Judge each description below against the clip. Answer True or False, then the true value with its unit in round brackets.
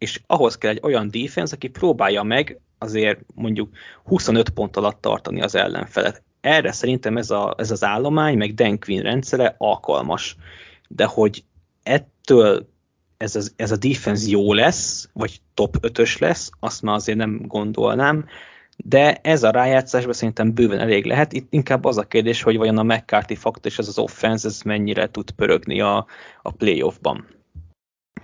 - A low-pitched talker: True (110 Hz)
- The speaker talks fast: True (165 wpm)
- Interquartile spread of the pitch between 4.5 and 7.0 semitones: False (2.9 semitones)